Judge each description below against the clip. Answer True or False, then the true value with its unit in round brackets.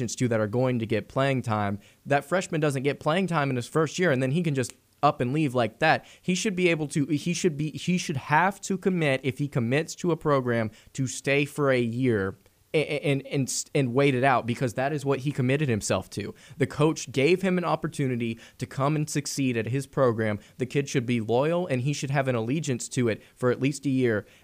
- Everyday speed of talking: False (240 wpm)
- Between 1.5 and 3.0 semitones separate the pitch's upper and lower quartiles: False (3.9 semitones)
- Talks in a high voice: False (135 Hz)